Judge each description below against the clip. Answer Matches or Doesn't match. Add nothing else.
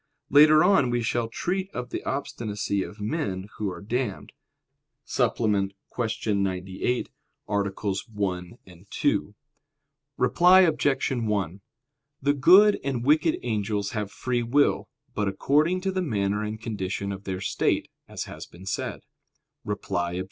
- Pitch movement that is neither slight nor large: Doesn't match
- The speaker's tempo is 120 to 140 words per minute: Matches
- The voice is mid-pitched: Doesn't match